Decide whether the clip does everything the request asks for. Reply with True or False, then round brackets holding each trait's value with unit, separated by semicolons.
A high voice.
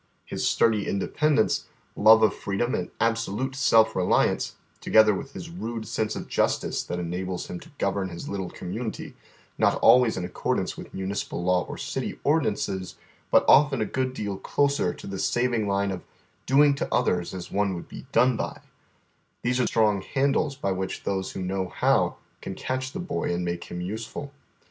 False (105 Hz)